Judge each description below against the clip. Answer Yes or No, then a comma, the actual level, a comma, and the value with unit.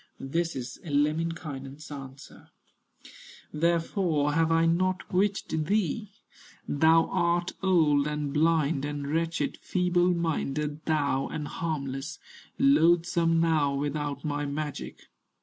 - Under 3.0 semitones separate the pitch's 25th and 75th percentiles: Yes, narrow, 2.6 semitones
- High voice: No, medium, 155 Hz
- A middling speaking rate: No, slow, 105 wpm